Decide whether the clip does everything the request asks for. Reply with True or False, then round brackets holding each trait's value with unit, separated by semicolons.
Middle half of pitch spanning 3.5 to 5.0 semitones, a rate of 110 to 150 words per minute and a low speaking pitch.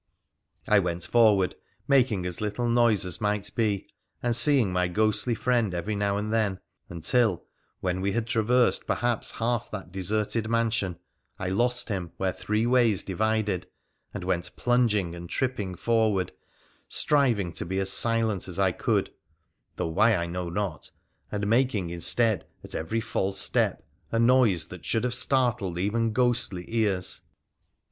False (4.0 semitones; 160 wpm; 105 Hz)